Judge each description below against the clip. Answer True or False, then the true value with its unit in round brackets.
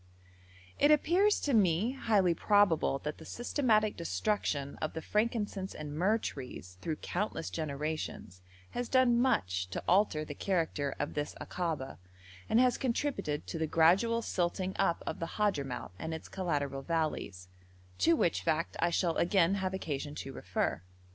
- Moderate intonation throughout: False (6.0 semitones)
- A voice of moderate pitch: True (170 Hz)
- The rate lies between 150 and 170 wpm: True (155 wpm)